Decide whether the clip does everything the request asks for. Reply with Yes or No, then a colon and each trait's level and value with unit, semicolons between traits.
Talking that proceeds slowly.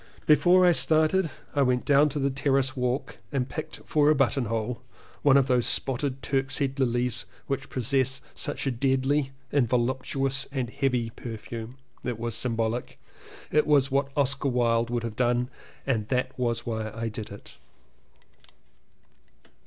No: average, 150 wpm